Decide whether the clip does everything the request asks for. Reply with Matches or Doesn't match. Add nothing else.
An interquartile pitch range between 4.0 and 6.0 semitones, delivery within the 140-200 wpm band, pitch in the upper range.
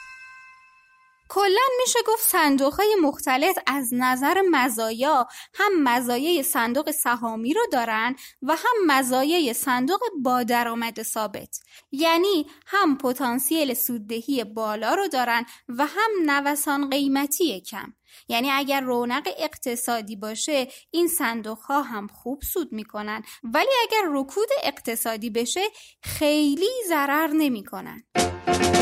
Doesn't match